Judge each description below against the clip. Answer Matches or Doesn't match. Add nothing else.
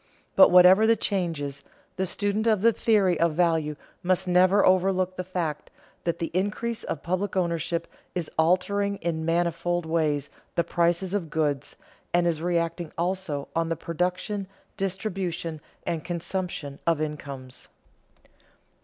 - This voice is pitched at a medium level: Matches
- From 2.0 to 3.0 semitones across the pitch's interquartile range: Matches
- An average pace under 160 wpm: Matches